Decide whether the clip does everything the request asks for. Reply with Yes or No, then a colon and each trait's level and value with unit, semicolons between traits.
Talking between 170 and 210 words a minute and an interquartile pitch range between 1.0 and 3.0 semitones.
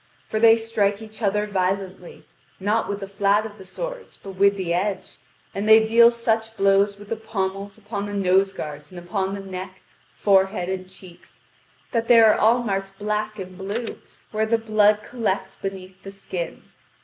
Yes: average, 180 wpm; narrow, 2.4 semitones